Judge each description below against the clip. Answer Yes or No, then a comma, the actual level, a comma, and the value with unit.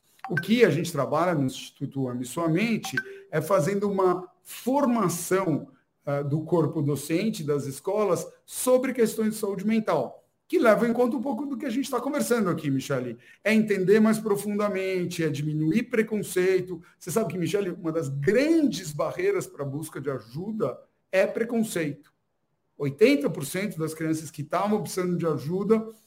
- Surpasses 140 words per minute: Yes, average, 155 wpm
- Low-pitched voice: No, medium, 185 Hz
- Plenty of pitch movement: Yes, wide, 5.9 semitones